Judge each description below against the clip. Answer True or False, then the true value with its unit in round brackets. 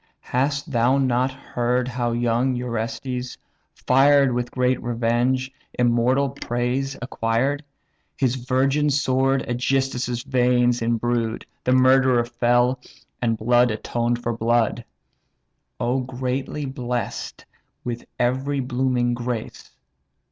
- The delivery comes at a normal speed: False (105 wpm)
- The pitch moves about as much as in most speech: False (1.6 semitones)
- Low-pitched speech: True (125 Hz)